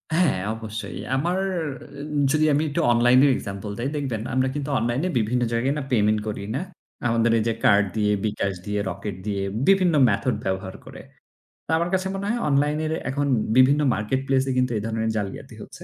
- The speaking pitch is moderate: No, low, 125 Hz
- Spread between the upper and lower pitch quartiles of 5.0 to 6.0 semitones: Yes, average, 5.3 semitones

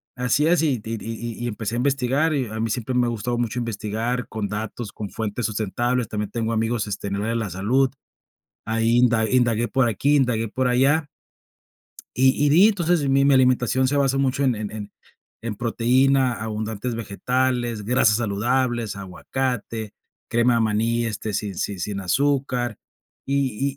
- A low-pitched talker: Yes, low, 120 Hz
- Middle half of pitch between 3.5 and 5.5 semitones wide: No, average, 3.0 semitones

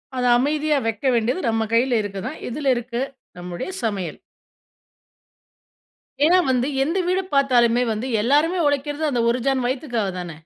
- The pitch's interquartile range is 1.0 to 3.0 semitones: No, average, 4.2 semitones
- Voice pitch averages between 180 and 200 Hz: No, very high, 250 Hz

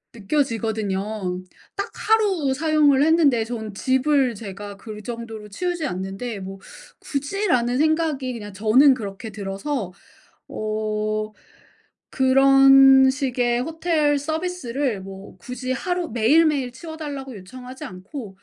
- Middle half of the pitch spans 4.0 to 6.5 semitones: Yes, average, 5.3 semitones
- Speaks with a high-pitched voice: Yes, very high, 255 Hz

